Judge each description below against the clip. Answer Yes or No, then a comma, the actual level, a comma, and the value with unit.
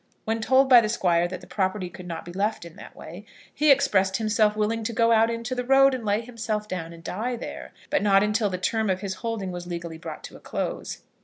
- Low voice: No, high, 210 Hz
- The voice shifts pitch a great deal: No, average, 3.9 semitones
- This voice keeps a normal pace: No, fast, 245 wpm